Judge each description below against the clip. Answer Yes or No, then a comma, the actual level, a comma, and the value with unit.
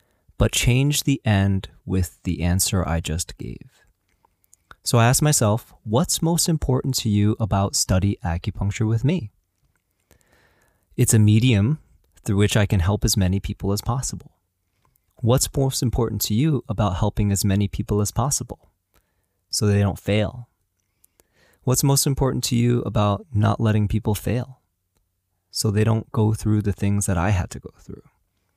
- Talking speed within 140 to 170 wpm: Yes, average, 160 wpm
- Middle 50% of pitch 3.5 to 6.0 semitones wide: Yes, average, 4.0 semitones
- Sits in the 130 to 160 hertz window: No, low, 105 Hz